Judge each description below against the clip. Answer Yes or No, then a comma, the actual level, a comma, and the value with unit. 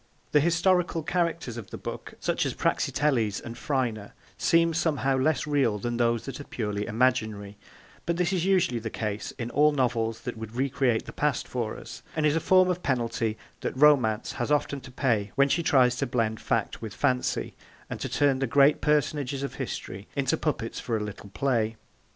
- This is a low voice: Yes, low, 130 Hz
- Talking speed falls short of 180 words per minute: No, average, 190 wpm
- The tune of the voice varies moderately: Yes, average, 4.7 semitones